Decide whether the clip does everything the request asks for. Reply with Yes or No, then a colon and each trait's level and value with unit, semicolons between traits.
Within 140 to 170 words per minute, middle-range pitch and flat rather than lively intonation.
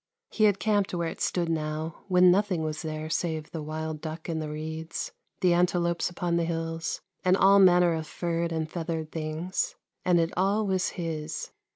No: average, 185 wpm; medium, 165 Hz; narrow, 2.2 semitones